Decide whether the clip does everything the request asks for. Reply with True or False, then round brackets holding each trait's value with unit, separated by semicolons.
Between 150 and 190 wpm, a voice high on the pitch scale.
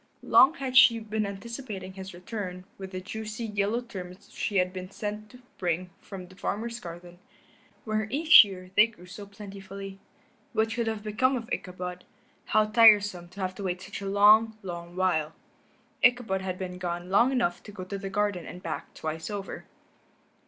True (180 wpm; 200 Hz)